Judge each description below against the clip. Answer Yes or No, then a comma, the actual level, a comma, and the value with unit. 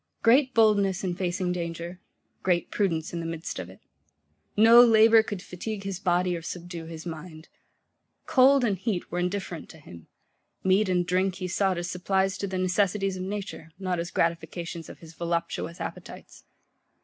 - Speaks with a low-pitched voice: No, medium, 180 Hz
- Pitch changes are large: No, average, 2.7 semitones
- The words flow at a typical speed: Yes, average, 170 wpm